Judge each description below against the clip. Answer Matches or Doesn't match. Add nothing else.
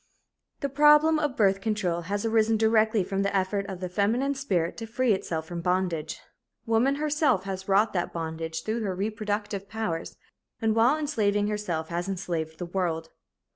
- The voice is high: Matches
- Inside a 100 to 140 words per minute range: Doesn't match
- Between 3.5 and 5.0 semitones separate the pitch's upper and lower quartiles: Matches